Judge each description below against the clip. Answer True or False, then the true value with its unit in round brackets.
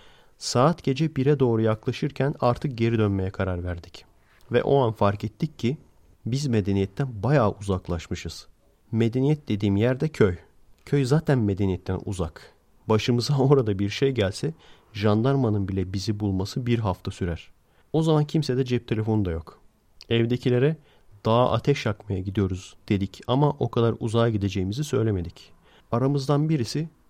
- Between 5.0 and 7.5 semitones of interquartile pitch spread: True (5.5 semitones)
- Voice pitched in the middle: False (115 Hz)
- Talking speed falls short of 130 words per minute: False (135 wpm)